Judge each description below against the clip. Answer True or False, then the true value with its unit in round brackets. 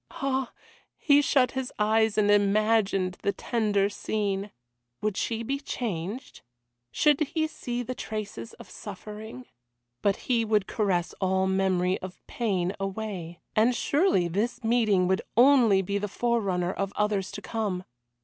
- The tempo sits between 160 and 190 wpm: False (140 wpm)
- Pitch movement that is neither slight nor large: True (3.6 semitones)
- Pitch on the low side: False (210 Hz)